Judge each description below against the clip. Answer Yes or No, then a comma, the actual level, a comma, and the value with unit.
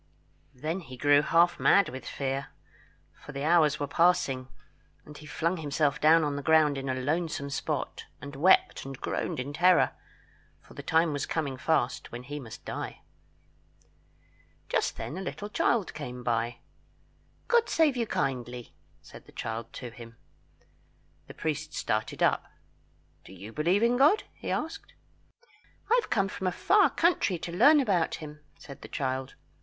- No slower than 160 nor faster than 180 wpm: Yes, average, 165 wpm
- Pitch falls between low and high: Yes, medium, 150 Hz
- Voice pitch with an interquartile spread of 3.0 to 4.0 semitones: No, average, 5.1 semitones